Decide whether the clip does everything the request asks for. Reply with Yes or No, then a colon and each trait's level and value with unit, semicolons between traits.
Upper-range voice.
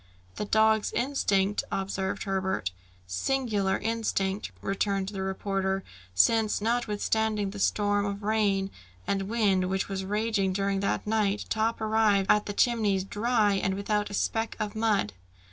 Yes: high, 205 Hz